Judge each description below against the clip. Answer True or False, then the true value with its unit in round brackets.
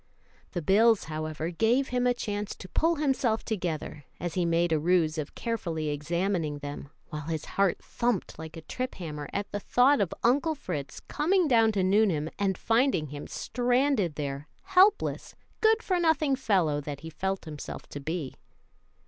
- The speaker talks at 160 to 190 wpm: True (170 wpm)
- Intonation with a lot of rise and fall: True (7.9 semitones)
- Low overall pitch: False (190 Hz)